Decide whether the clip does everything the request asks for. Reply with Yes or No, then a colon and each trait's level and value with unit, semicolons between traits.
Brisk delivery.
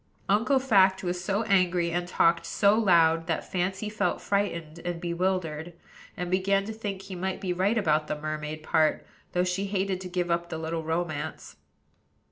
No: average, 175 wpm